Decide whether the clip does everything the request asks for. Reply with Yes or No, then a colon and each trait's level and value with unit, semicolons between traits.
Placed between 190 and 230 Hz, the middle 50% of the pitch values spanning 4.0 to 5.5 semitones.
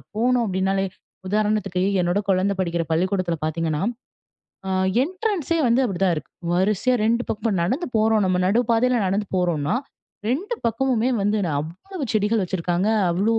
Yes: high, 200 Hz; average, 4.5 semitones